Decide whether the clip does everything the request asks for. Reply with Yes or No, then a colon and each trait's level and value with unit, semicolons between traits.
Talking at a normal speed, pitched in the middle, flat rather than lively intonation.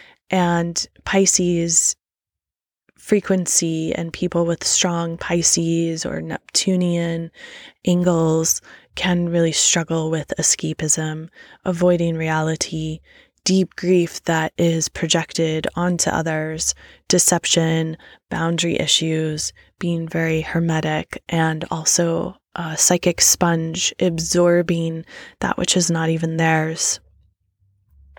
No: slow, 90 wpm; medium, 165 Hz; narrow, 1.6 semitones